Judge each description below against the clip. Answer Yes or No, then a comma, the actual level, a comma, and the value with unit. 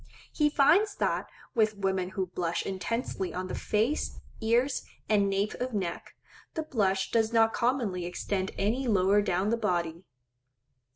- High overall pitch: Yes, high, 210 Hz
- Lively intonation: No, average, 3.8 semitones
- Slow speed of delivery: No, average, 150 wpm